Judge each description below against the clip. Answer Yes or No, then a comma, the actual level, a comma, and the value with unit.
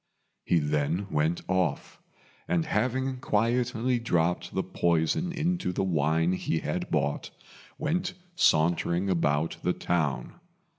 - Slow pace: Yes, slow, 115 wpm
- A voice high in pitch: No, very low, 90 Hz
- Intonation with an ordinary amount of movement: No, wide, 7.3 semitones